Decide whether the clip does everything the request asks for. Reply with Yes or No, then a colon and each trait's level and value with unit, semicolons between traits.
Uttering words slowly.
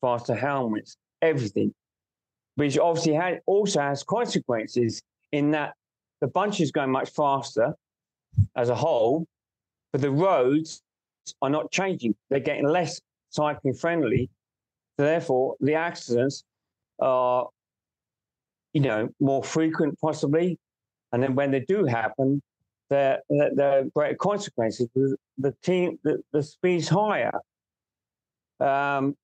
Yes: slow, 120 wpm